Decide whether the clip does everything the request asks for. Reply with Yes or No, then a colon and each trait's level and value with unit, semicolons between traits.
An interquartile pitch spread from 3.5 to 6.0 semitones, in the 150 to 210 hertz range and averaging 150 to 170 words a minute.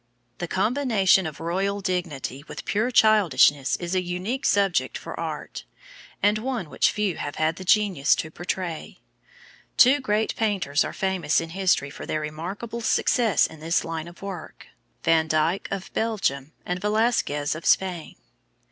Yes: average, 4.6 semitones; medium, 185 Hz; average, 155 wpm